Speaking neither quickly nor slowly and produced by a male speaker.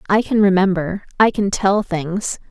No: average, 170 wpm; female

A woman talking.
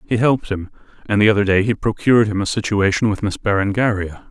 No: male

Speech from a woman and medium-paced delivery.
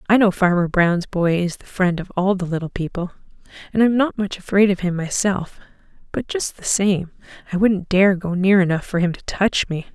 No: female; fast, 215 wpm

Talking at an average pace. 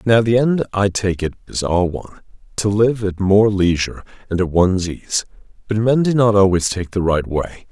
No: fast, 210 wpm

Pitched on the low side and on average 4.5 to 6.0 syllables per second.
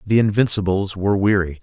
Yes: low, 100 Hz; 5.9 syllables/s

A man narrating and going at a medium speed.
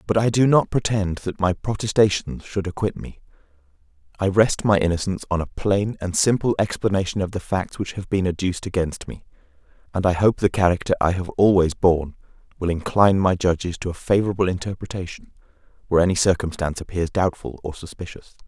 Yes: male; average, 175 wpm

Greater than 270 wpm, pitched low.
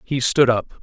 No: fast, 215 wpm; low, 125 Hz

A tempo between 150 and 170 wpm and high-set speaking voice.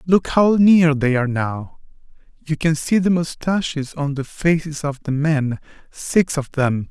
No: average, 165 wpm; medium, 150 Hz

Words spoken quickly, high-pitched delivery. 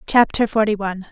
No: average, 160 wpm; high, 210 Hz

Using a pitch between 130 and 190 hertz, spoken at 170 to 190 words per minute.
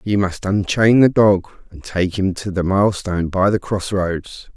No: very low, 95 Hz; average, 185 wpm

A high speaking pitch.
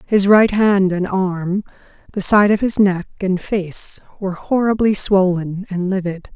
Yes: high, 195 Hz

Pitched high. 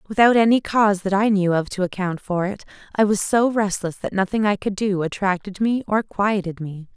Yes: high, 200 Hz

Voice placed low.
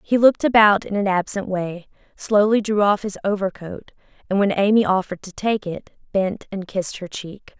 No: high, 200 Hz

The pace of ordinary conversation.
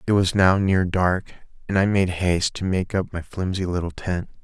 No: fast, 215 wpm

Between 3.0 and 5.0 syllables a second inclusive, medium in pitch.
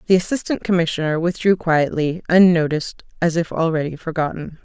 No: 5.7 syllables/s; medium, 165 Hz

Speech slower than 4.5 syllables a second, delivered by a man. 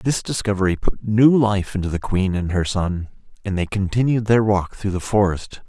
No: 5.0 syllables/s; male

